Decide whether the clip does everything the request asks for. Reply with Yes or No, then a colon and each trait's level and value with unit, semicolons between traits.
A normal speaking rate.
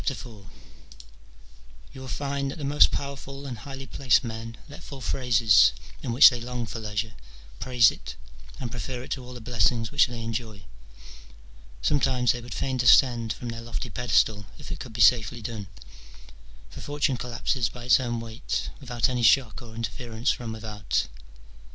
Yes: average, 170 wpm